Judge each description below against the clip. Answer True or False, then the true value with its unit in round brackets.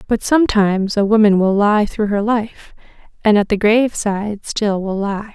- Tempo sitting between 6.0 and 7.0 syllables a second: False (4.9 syllables/s)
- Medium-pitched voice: False (210 Hz)